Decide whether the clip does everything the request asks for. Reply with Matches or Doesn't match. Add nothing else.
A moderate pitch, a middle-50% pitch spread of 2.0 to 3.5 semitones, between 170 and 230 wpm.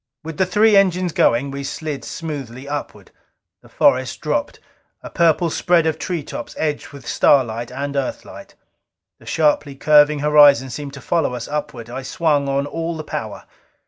Doesn't match